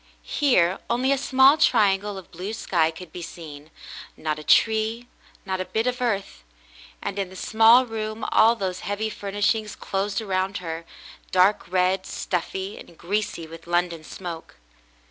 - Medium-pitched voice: No, high, 195 Hz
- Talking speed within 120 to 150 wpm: No, average, 165 wpm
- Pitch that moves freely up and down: No, average, 4.0 semitones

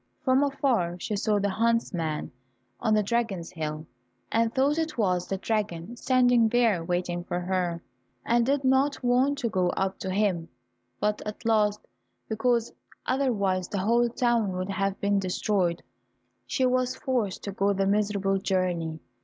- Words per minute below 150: No, average, 155 wpm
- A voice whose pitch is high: Yes, high, 210 Hz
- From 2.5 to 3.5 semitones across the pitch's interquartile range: No, average, 4.5 semitones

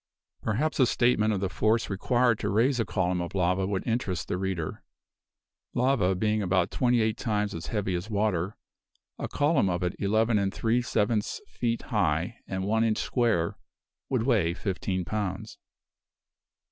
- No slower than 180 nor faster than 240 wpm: No, average, 160 wpm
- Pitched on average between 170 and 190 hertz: No, low, 105 Hz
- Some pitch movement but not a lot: Yes, average, 3.6 semitones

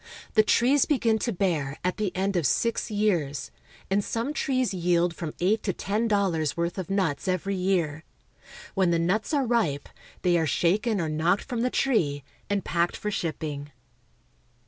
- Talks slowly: No, average, 170 wpm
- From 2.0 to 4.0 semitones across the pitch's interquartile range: No, average, 4.4 semitones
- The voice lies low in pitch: No, medium, 185 Hz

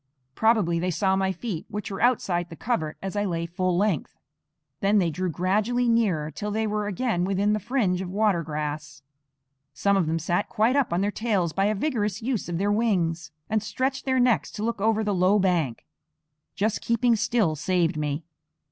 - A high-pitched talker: Yes, high, 195 Hz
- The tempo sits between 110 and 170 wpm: No, average, 195 wpm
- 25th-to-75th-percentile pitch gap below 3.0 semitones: No, average, 4.1 semitones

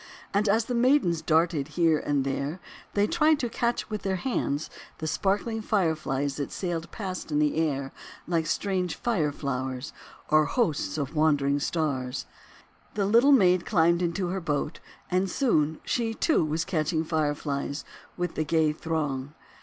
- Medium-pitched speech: Yes, medium, 165 Hz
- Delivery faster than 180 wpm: No, average, 155 wpm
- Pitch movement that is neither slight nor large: Yes, average, 5.0 semitones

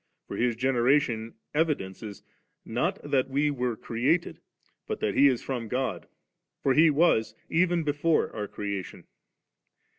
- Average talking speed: No, slow, 130 wpm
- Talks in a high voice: No, low, 130 Hz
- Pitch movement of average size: Yes, average, 4.8 semitones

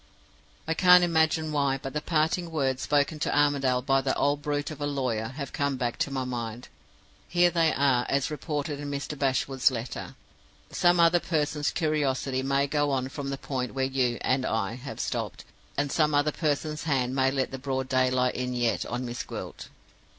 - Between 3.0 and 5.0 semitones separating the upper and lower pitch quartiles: No, narrow, 2.6 semitones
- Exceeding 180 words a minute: Yes, average, 190 wpm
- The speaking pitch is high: No, medium, 140 Hz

